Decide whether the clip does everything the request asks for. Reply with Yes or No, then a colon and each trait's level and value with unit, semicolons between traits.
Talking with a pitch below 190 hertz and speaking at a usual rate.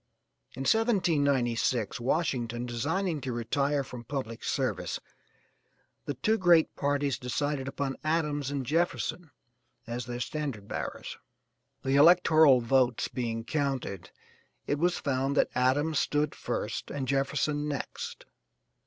No: medium, 140 Hz; slow, 120 wpm